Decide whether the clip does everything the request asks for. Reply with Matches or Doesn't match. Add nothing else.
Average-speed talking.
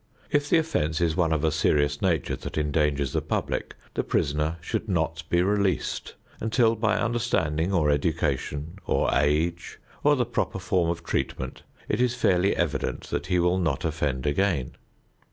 Matches